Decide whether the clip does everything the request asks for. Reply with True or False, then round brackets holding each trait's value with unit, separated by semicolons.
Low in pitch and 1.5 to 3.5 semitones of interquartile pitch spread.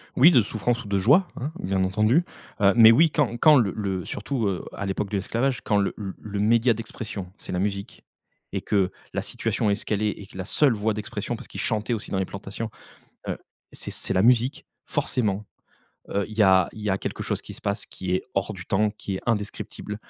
True (105 Hz; 2.9 semitones)